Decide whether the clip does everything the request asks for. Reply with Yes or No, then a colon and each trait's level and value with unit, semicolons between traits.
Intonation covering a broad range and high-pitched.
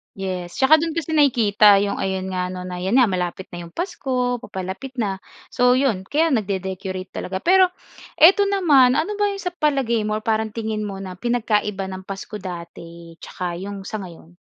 Yes: wide, 6.1 semitones; high, 210 Hz